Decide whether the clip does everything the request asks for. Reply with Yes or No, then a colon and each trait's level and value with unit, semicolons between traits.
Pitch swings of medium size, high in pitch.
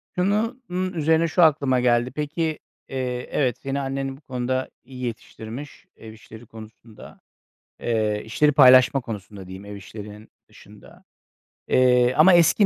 No: average, 5.0 semitones; low, 130 Hz